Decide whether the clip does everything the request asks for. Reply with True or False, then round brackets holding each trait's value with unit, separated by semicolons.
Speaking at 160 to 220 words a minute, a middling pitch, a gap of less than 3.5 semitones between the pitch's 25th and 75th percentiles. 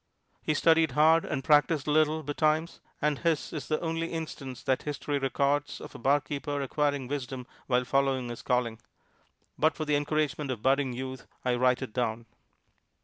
True (170 wpm; 145 Hz; 2.9 semitones)